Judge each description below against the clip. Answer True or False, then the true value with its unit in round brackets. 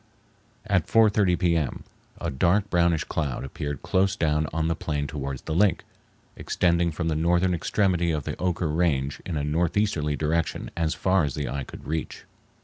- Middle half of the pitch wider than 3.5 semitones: False (2.8 semitones)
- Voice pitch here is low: True (80 Hz)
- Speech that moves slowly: False (170 wpm)